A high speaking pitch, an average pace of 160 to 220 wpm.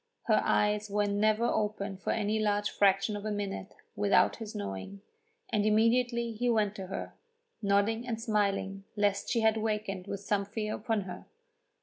Yes: high, 210 Hz; average, 165 wpm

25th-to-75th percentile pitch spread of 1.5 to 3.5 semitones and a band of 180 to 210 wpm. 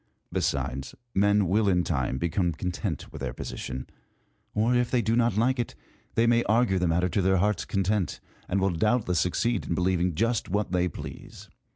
No: average, 4.0 semitones; average, 190 wpm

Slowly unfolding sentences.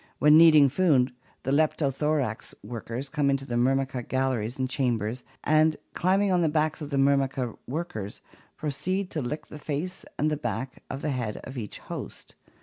No: average, 175 wpm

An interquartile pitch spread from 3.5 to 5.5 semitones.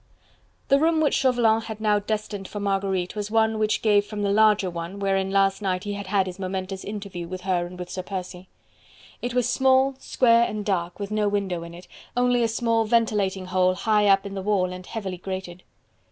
No: average, 2.8 semitones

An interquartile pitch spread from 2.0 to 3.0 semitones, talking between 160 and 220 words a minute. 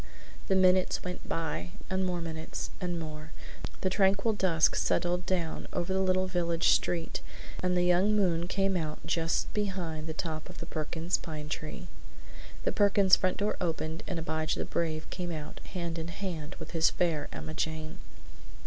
Yes: average, 2.7 semitones; average, 170 wpm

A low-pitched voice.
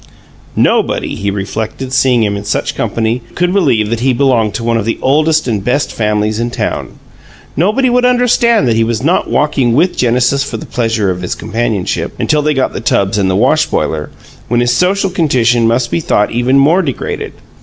Yes: low, 120 Hz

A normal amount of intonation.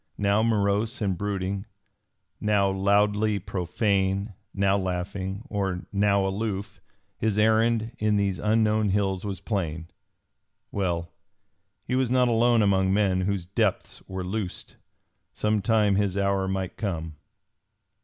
No: narrow, 2.0 semitones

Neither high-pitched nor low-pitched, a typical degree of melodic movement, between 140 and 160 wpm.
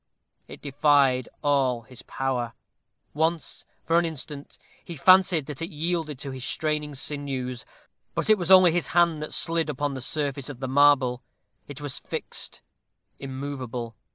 Yes: medium, 145 Hz; average, 3.5 semitones; average, 155 wpm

